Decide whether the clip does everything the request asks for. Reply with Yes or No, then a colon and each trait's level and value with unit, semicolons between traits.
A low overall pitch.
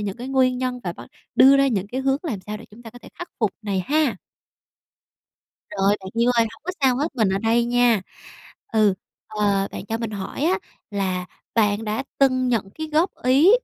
No: high, 230 Hz